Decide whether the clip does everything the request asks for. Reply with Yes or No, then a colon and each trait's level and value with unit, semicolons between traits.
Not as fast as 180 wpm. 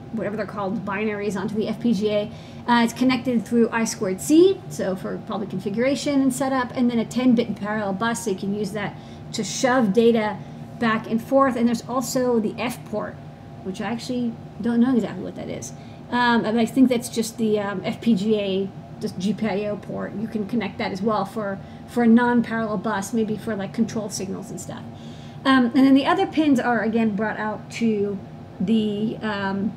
No: average, 190 wpm